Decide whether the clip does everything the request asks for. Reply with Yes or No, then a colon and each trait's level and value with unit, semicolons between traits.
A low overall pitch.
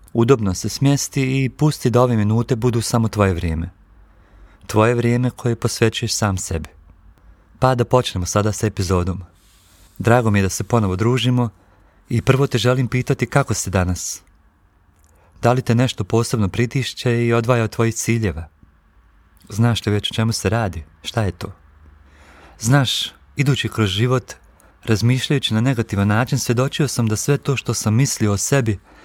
Yes: low, 110 Hz